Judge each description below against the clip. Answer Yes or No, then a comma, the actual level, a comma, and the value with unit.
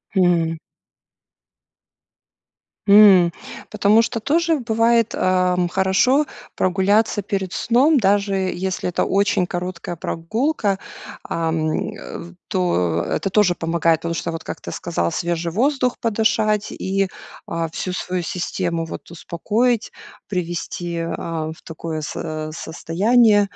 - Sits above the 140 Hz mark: Yes, medium, 185 Hz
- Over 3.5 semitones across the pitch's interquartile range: Yes, average, 4.0 semitones